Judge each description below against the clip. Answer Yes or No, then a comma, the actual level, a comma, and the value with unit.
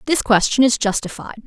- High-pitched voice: Yes, high, 235 Hz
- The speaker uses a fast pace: No, average, 165 wpm